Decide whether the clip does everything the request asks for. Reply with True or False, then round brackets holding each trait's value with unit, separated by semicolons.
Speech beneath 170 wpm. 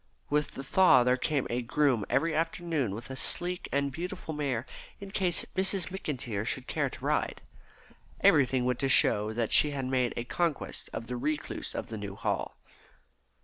False (180 wpm)